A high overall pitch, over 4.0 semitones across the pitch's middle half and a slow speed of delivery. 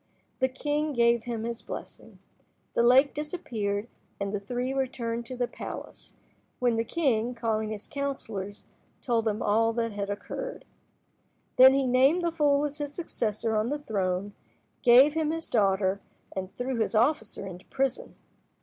No: high, 235 Hz; average, 4.4 semitones; average, 160 wpm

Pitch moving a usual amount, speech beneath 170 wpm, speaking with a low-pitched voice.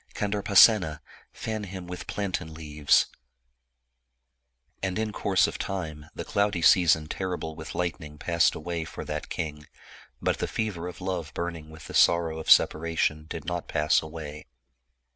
Yes: average, 3.2 semitones; average, 150 wpm; very low, 85 Hz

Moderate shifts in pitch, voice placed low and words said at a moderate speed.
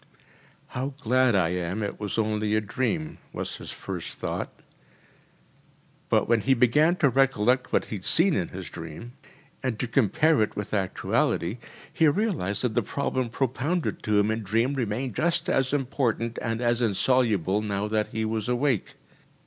Yes: average, 4.1 semitones; low, 115 Hz; average, 170 wpm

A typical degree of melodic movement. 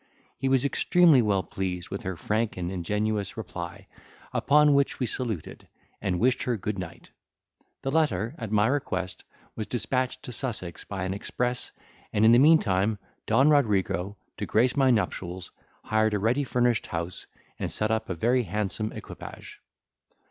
Yes: average, 4.8 semitones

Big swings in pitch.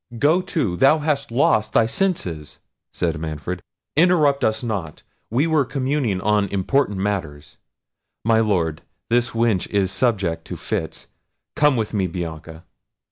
Yes: wide, 7.5 semitones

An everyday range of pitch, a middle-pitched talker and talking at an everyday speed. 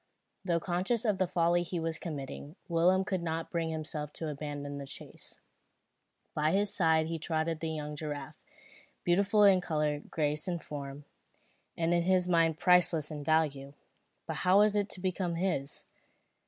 Yes: average, 3.2 semitones; medium, 165 Hz; average, 160 wpm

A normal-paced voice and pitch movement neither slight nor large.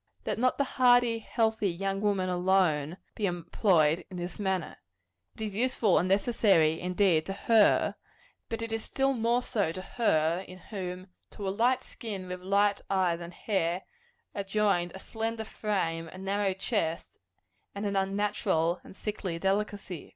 Yes: average, 160 wpm; average, 3.2 semitones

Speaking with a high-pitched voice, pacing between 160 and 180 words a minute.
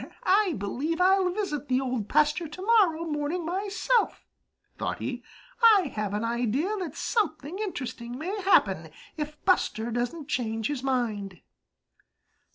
No: very high, 300 Hz; slow, 135 wpm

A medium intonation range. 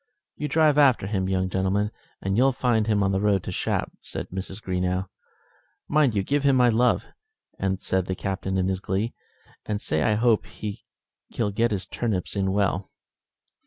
Yes: average, 3.8 semitones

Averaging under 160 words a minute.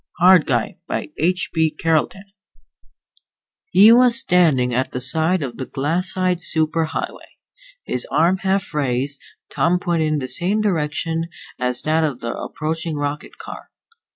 Yes: average, 150 wpm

